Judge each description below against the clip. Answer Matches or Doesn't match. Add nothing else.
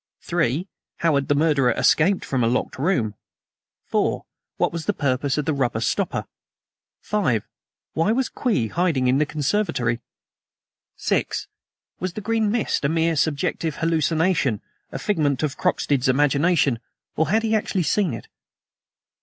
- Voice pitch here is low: Doesn't match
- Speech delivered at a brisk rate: Doesn't match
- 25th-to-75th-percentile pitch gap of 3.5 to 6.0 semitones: Matches